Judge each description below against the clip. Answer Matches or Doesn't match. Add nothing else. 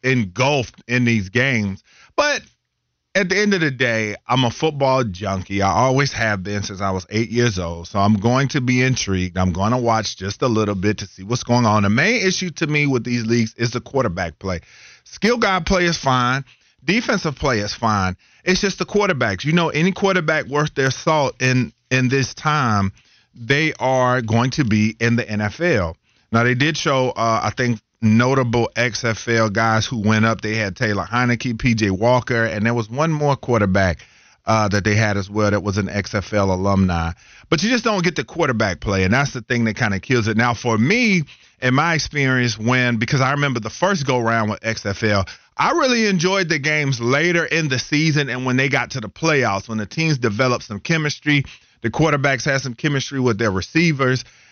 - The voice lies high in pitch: Doesn't match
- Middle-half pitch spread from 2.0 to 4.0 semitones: Doesn't match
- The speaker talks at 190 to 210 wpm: Matches